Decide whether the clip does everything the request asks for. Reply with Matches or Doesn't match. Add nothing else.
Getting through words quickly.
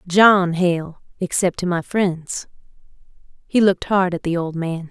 Doesn't match